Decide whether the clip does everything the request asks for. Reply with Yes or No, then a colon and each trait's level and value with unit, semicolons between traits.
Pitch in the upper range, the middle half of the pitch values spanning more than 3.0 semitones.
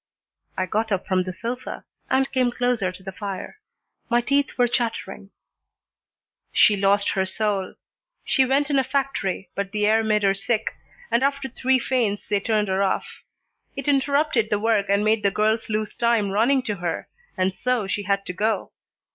Yes: high, 215 Hz; average, 4.1 semitones